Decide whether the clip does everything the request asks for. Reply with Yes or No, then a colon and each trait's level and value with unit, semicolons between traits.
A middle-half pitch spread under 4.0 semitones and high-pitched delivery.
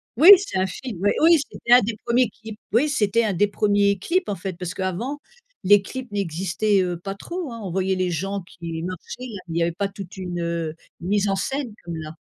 No: average, 4.3 semitones; high, 195 Hz